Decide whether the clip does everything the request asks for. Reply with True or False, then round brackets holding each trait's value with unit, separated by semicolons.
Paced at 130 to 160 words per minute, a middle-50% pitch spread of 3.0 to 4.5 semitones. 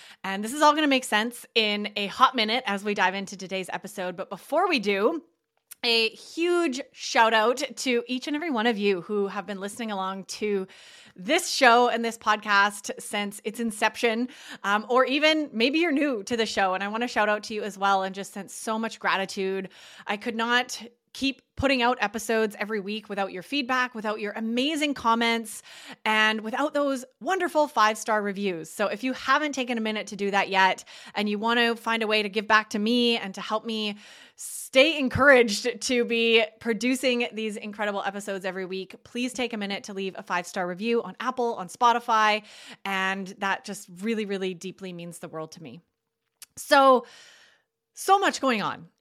False (200 wpm; 3.7 semitones)